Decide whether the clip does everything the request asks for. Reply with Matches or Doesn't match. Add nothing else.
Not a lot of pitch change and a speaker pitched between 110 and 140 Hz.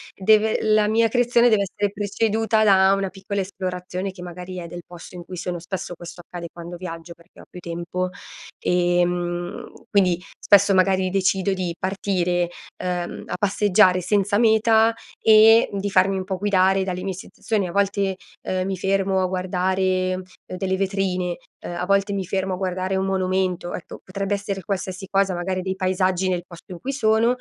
Doesn't match